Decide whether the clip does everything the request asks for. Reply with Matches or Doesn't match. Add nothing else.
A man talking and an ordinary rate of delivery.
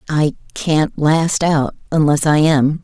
Doesn't match